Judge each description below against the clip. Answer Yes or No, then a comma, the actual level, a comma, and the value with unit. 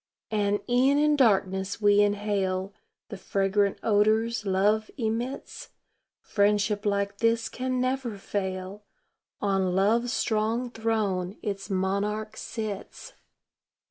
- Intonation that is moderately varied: No, narrow, 2.3 semitones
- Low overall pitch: No, high, 210 Hz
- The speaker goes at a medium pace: No, slow, 105 wpm